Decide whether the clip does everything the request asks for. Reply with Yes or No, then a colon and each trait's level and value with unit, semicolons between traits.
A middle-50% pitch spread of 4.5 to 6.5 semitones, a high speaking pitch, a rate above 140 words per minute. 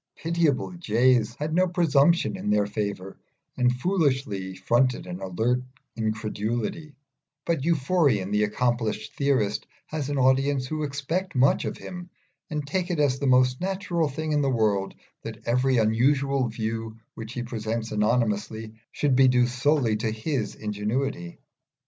No: average, 4.9 semitones; low, 125 Hz; average, 150 wpm